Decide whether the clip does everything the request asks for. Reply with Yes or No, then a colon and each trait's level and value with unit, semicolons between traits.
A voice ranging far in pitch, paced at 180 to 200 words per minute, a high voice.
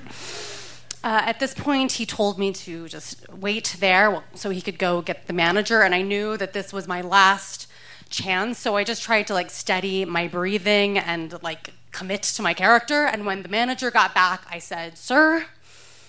No: average, 3.2 semitones; average, 195 wpm; high, 195 Hz